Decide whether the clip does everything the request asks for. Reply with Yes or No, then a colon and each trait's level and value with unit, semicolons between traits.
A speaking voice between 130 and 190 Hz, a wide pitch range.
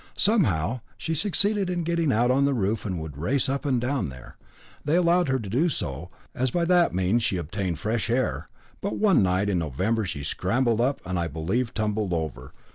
No: low, 115 Hz; wide, 7.8 semitones